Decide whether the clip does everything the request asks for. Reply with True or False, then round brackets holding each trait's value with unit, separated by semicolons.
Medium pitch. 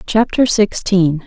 False (200 Hz)